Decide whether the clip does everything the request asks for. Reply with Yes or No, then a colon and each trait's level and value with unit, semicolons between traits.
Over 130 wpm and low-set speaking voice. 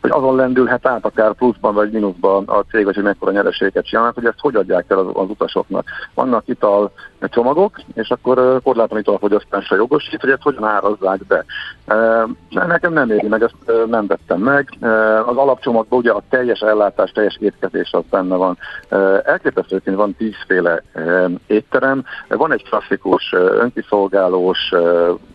Yes: average, 150 wpm; low, 110 Hz